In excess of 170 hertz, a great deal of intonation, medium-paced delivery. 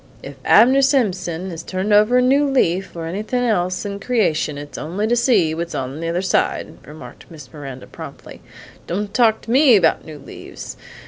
Yes: high, 190 Hz; wide, 6.3 semitones; average, 180 wpm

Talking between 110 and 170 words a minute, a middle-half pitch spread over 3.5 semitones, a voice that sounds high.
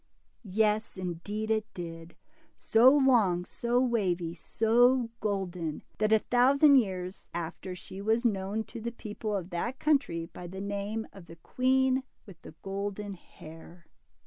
Yes: average, 145 wpm; average, 4.8 semitones; high, 205 Hz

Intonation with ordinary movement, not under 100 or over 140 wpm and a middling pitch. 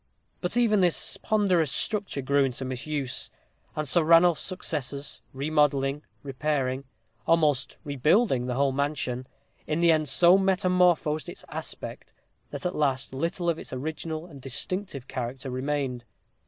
Yes: average, 4.3 semitones; slow, 135 wpm; medium, 150 Hz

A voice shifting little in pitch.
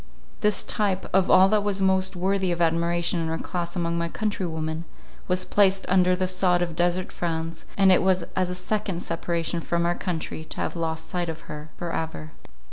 Yes: narrow, 2.0 semitones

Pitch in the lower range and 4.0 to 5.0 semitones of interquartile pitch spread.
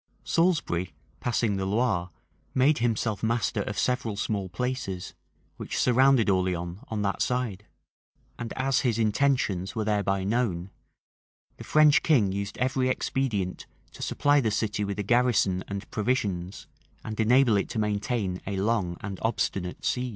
Yes: low, 110 Hz; average, 4.3 semitones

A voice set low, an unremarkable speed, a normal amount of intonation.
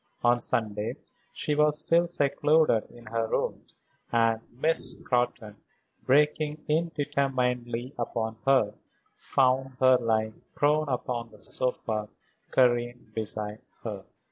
No: low, 125 Hz; slow, 115 wpm; average, 4.2 semitones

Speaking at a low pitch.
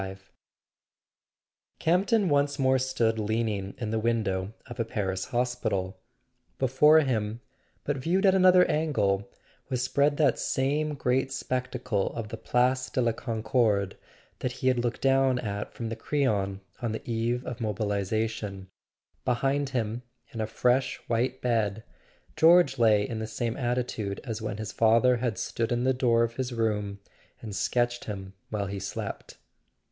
Yes: low, 120 Hz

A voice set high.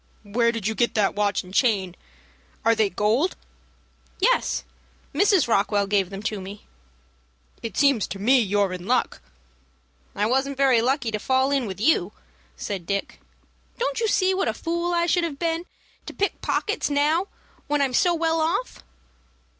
Yes: very high, 250 Hz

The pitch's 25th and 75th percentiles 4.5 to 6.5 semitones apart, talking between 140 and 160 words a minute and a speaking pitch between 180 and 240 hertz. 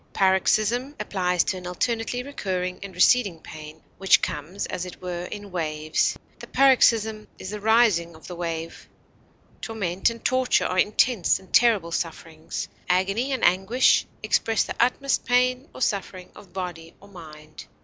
Yes: average, 4.8 semitones; average, 150 wpm; high, 190 Hz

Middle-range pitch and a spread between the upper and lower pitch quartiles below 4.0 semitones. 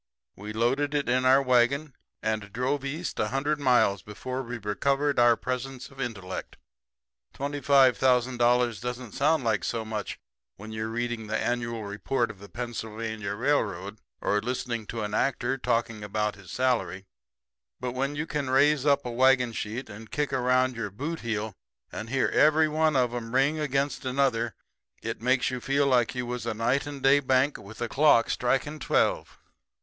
No: low, 125 Hz; average, 3.4 semitones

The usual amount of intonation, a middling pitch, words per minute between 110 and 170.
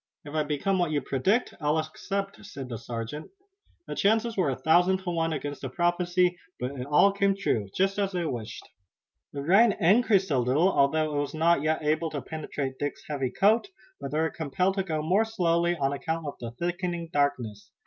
No: average, 4.7 semitones; medium, 160 Hz; average, 200 wpm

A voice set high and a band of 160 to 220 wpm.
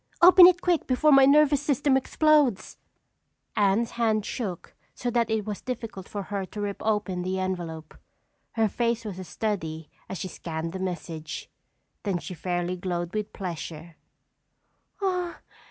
No: high, 205 Hz; average, 150 wpm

